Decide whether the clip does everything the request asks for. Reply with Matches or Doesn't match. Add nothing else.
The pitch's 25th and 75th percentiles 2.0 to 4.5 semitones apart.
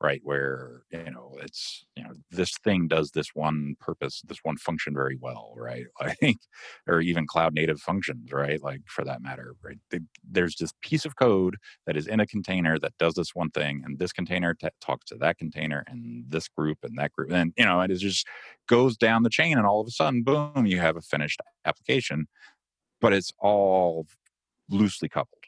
Doesn't match